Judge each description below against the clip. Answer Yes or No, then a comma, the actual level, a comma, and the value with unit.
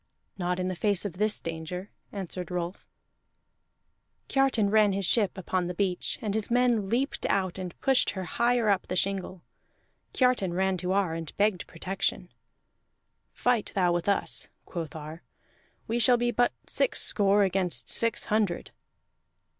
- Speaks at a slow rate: No, average, 155 wpm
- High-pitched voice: Yes, high, 195 Hz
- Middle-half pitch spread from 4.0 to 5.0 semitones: No, average, 3.3 semitones